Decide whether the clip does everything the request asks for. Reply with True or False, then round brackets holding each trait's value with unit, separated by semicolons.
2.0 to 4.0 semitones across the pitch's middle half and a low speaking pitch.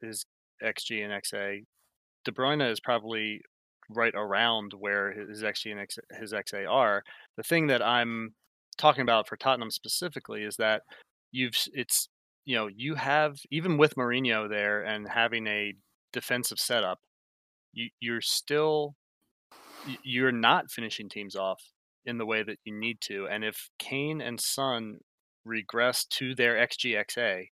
True (3.5 semitones; 115 Hz)